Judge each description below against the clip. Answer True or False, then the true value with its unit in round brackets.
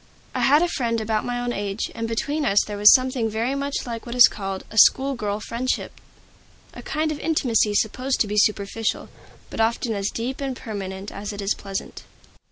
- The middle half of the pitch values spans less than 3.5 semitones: False (3.8 semitones)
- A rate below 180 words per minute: False (200 wpm)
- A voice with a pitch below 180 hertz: False (225 Hz)